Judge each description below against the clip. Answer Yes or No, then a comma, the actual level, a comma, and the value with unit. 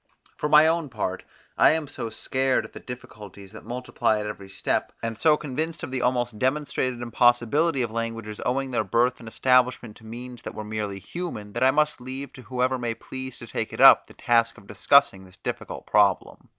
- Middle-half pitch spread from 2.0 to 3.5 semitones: Yes, average, 3.2 semitones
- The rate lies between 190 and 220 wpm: Yes, fast, 205 wpm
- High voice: No, low, 125 Hz